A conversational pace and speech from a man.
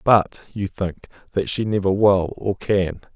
Yes: average, 170 wpm; male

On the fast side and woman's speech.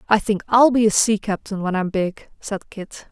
Yes: fast, 230 wpm; female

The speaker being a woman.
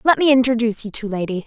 Yes: female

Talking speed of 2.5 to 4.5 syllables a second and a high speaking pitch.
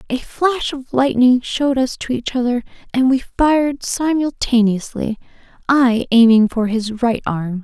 Yes: 4.3 syllables/s; very high, 250 Hz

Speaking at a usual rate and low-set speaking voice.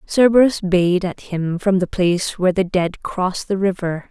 No: average, 190 wpm; medium, 185 Hz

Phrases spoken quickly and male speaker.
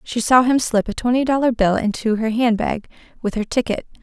No: fast, 210 wpm; female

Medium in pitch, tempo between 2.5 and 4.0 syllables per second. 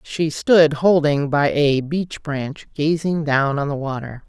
Yes: medium, 150 Hz; 3.7 syllables/s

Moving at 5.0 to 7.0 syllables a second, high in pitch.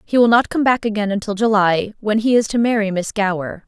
Yes: 5.8 syllables/s; high, 210 Hz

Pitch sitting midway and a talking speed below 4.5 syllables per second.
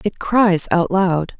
Yes: medium, 180 Hz; 4.0 syllables/s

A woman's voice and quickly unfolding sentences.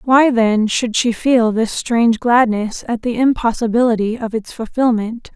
No: female; average, 155 wpm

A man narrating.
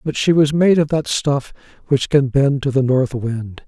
Yes: male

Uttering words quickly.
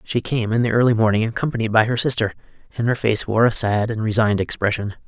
Yes: fast, 225 wpm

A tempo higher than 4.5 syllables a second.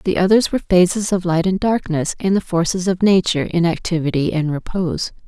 Yes: 5.8 syllables/s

